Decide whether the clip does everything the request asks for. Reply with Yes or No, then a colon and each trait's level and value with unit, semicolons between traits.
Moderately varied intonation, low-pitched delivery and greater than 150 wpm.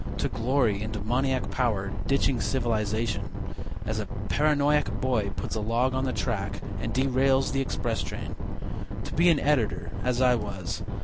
Yes: average, 3.7 semitones; low, 120 Hz; average, 160 wpm